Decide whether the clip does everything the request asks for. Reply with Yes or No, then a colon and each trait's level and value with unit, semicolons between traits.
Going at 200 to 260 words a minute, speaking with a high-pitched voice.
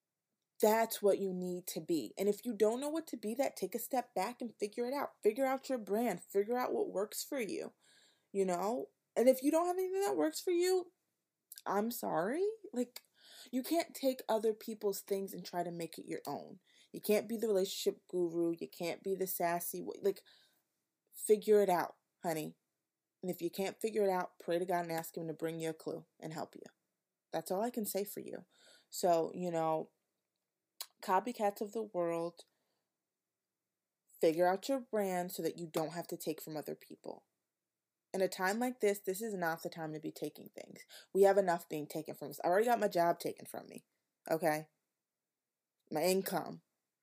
Yes: fast, 205 wpm; high, 195 Hz